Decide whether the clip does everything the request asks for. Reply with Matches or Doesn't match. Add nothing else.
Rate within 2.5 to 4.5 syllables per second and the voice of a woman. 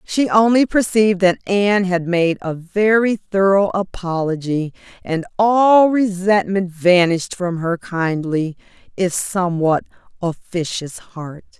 Matches